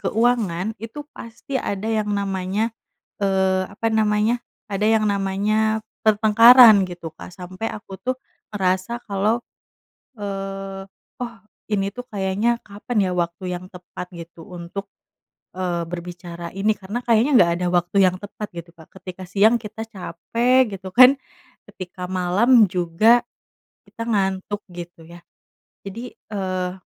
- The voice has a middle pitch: No, high, 195 Hz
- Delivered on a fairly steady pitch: No, average, 3.3 semitones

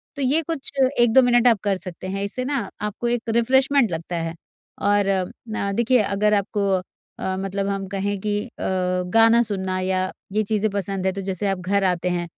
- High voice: Yes, high, 200 Hz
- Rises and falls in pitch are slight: No, average, 3.3 semitones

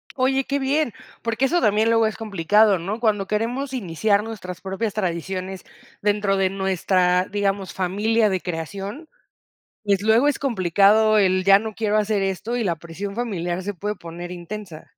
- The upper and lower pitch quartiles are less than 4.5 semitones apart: Yes, average, 3.0 semitones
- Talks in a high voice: Yes, high, 205 Hz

